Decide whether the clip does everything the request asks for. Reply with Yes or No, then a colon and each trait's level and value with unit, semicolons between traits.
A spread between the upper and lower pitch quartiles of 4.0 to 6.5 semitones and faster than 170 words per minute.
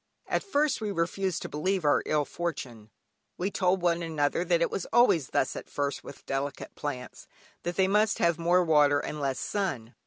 Yes: average, 4.7 semitones; average, 190 wpm